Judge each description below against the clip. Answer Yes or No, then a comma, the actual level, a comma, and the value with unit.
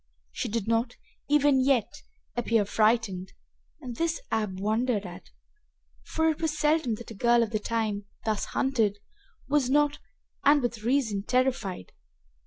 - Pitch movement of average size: Yes, average, 4.4 semitones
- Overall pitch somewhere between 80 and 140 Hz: No, high, 235 Hz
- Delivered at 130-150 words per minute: Yes, average, 145 wpm